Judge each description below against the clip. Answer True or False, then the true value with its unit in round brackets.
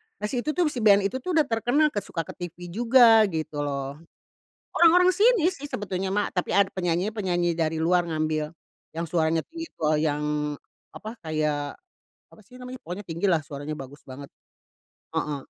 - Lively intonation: True (7.0 semitones)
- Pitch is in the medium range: True (180 Hz)